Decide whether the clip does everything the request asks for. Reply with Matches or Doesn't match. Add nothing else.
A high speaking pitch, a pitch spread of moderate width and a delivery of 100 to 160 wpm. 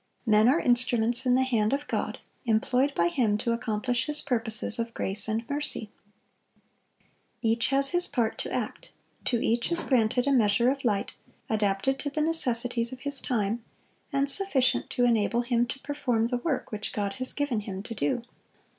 Doesn't match